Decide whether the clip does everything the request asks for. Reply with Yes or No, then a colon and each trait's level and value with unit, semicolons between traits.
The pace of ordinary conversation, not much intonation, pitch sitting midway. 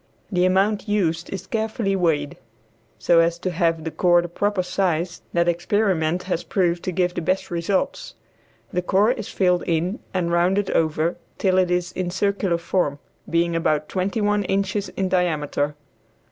Yes: average, 165 wpm; narrow, 2.3 semitones; medium, 180 Hz